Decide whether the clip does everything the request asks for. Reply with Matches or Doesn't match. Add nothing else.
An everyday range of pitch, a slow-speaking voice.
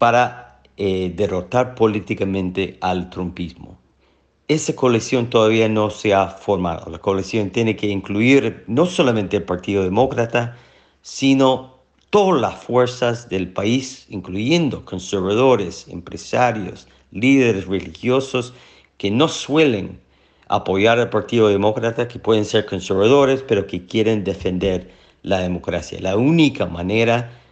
Matches